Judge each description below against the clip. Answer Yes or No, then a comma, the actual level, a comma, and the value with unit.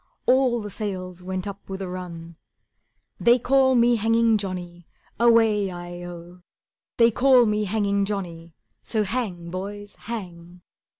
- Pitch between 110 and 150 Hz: No, high, 200 Hz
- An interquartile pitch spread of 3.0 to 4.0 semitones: No, average, 4.4 semitones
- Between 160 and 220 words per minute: No, slow, 135 wpm